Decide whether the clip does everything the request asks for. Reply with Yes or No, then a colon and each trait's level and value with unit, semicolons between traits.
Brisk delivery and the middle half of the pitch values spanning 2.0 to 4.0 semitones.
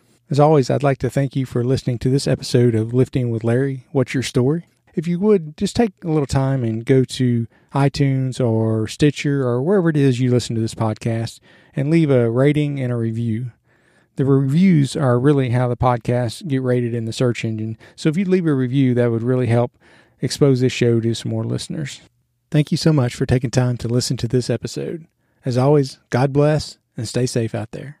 Yes: fast, 215 wpm; average, 3.1 semitones